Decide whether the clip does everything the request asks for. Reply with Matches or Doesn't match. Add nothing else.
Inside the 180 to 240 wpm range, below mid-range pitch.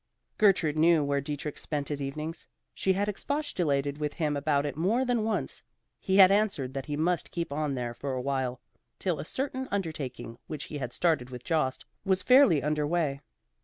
Doesn't match